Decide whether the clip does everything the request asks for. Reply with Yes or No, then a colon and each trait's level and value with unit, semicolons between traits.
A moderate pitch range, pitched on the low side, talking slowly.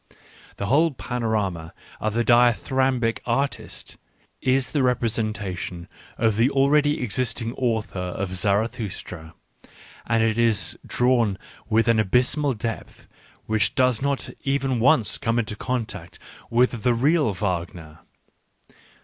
Yes: average, 3.5 semitones; low, 115 Hz; slow, 120 wpm